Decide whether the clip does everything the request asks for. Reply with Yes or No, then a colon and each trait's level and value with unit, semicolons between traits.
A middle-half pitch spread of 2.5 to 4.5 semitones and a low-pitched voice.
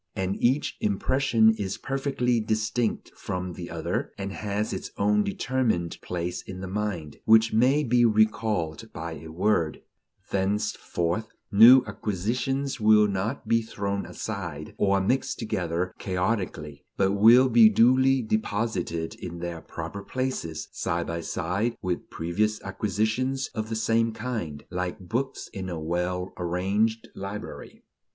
Yes: average, 3.9 semitones; low, 105 Hz